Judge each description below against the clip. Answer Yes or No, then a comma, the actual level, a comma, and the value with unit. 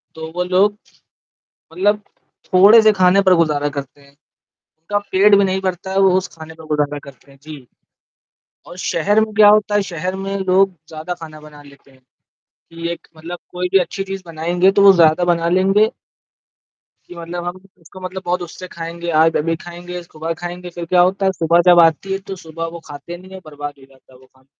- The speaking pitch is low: No, medium, 175 Hz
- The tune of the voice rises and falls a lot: No, average, 3.0 semitones